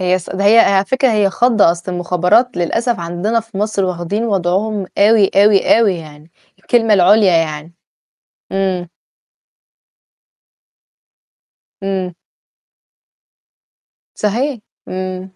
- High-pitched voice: Yes, high, 195 Hz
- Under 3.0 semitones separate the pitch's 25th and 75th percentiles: No, average, 3.4 semitones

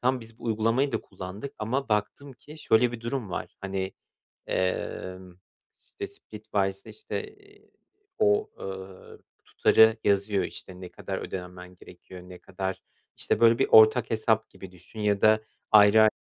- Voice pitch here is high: No, low, 110 Hz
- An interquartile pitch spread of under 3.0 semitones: No, average, 3.6 semitones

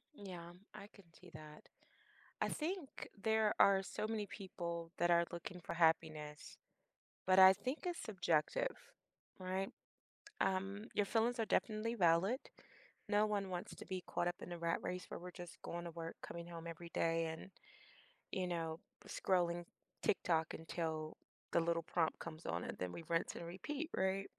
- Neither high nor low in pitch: Yes, medium, 175 Hz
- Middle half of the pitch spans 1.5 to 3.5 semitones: Yes, average, 3.1 semitones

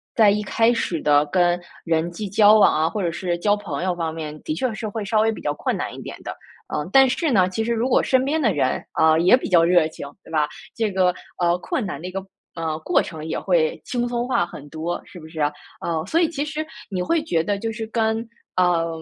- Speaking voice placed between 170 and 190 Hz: Yes, medium, 185 Hz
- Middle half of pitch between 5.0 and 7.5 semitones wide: Yes, wide, 5.5 semitones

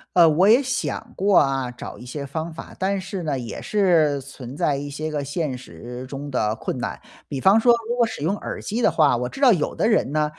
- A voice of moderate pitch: Yes, medium, 150 Hz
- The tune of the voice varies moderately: No, wide, 6.2 semitones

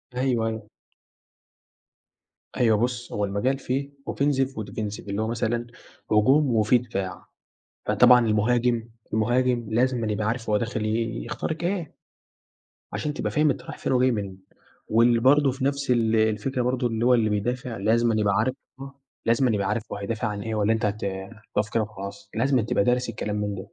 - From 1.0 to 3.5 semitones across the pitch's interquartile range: Yes, average, 2.9 semitones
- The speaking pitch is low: Yes, low, 115 Hz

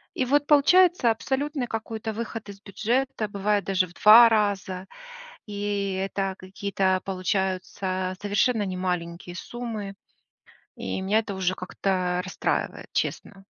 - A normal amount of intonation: Yes, average, 3.1 semitones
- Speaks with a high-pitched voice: Yes, high, 200 Hz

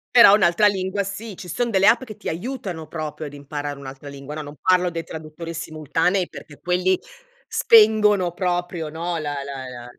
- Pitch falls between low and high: Yes, medium, 175 Hz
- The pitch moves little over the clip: No, average, 4.7 semitones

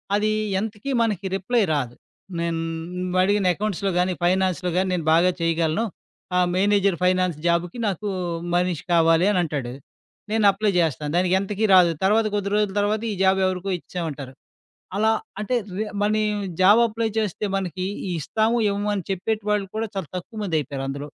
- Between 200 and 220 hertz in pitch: No, high, 190 Hz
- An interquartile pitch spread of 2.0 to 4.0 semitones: Yes, average, 3.4 semitones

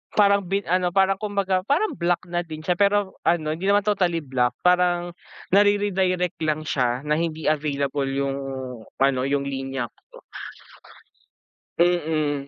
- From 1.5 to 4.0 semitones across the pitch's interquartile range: No, average, 4.9 semitones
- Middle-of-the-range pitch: Yes, medium, 175 Hz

